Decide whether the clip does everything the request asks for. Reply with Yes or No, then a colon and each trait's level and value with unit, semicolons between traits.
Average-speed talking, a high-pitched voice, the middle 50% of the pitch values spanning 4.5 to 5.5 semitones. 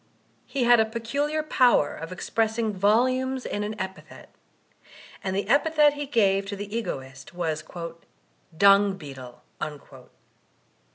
No: slow, 120 wpm; high, 210 Hz; average, 5.0 semitones